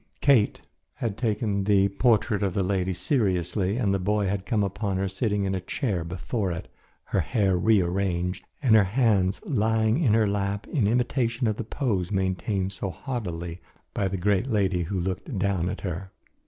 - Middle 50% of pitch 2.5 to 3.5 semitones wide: Yes, average, 2.9 semitones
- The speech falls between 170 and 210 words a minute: Yes, average, 180 wpm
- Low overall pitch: Yes, low, 100 Hz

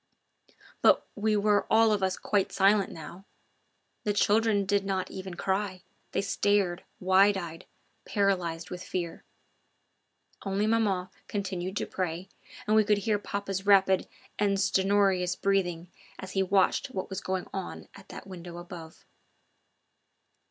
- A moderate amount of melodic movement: No, narrow, 1.8 semitones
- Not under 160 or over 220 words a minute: No, average, 140 wpm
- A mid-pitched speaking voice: No, high, 195 Hz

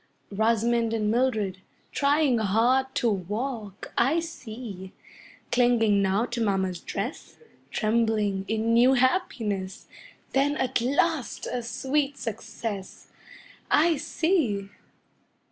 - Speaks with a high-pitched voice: Yes, high, 230 Hz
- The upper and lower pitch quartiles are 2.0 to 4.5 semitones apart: Yes, average, 4.2 semitones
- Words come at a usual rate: No, slow, 100 wpm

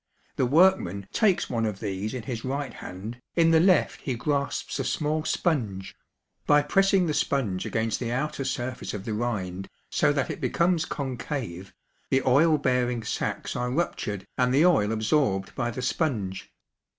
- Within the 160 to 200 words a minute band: Yes, average, 165 wpm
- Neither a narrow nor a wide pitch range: No, wide, 5.7 semitones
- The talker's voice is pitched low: Yes, low, 125 Hz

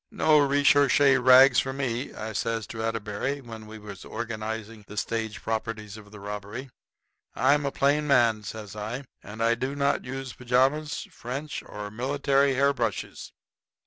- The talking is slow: No, average, 155 wpm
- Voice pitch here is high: No, low, 120 Hz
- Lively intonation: No, average, 4.1 semitones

